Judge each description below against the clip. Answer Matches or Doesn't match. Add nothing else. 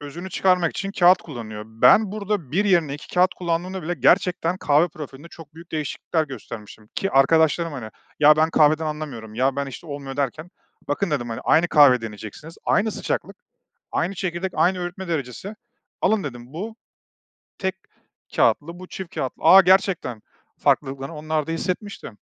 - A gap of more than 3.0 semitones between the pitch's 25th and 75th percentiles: Matches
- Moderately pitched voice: Matches